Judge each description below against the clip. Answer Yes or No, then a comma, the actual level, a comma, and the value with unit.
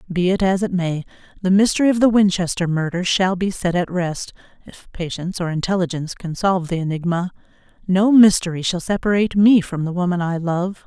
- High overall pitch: No, medium, 180 Hz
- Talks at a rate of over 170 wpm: Yes, average, 190 wpm